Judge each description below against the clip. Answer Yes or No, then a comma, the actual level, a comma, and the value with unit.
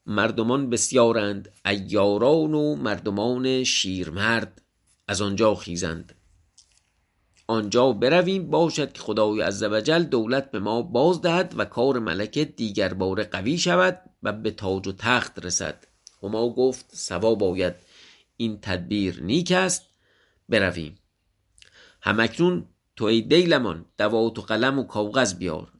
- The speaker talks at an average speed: No, slow, 125 wpm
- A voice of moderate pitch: No, low, 110 Hz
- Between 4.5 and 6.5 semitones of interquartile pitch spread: Yes, average, 5.3 semitones